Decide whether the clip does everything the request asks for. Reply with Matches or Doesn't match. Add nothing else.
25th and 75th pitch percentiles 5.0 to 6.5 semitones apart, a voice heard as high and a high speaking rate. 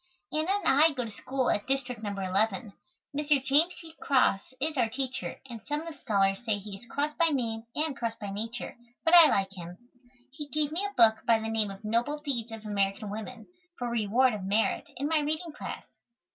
Matches